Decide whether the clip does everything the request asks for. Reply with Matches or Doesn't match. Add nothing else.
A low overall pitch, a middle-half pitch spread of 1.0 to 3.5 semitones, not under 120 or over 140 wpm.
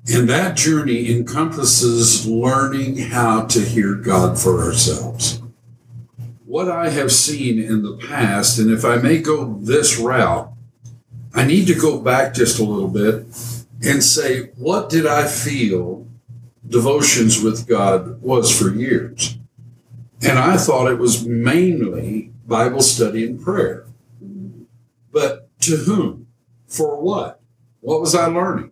Matches